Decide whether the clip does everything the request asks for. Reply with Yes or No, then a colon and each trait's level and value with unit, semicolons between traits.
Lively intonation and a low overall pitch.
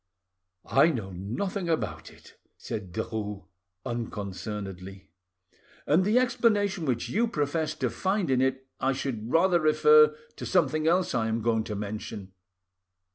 Yes: wide, 8.4 semitones; low, 130 Hz